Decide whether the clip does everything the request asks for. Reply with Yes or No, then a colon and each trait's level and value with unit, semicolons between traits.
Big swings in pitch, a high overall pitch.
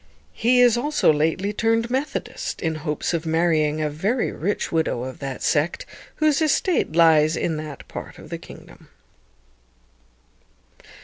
No: wide, 7.3 semitones; medium, 165 Hz